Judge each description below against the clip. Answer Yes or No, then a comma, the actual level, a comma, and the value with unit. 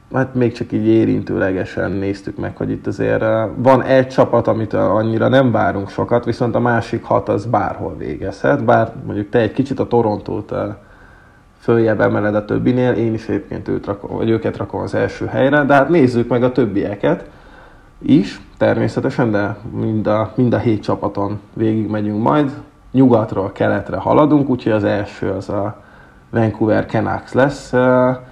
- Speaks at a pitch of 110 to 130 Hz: Yes, low, 115 Hz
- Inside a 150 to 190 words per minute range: Yes, fast, 155 wpm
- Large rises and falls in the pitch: No, average, 3.3 semitones